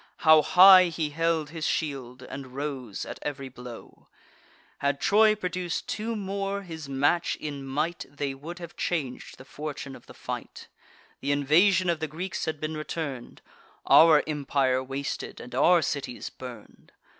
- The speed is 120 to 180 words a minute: Yes, average, 155 wpm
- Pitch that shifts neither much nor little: Yes, average, 4.0 semitones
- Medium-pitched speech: Yes, medium, 150 Hz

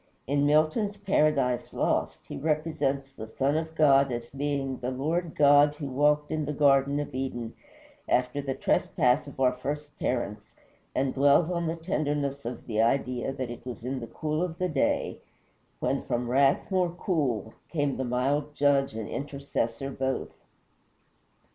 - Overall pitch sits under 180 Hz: Yes, medium, 140 Hz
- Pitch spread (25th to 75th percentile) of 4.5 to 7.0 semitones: No, average, 2.8 semitones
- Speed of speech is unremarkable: Yes, average, 160 wpm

